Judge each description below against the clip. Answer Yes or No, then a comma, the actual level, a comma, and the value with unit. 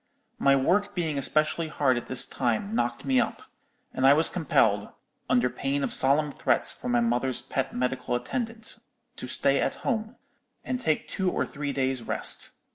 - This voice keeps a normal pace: Yes, average, 175 wpm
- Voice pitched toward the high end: No, medium, 140 Hz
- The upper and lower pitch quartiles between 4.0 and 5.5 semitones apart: Yes, average, 4.7 semitones